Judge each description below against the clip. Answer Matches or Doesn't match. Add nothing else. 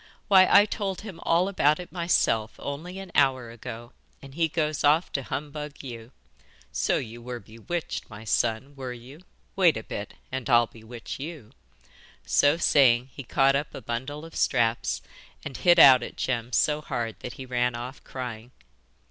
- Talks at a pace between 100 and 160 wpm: Doesn't match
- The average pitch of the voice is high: Doesn't match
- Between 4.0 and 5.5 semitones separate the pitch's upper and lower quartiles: Matches